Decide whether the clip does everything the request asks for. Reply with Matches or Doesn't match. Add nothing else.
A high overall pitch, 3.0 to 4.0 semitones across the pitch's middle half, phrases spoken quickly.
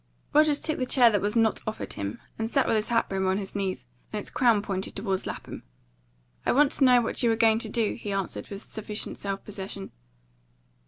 Matches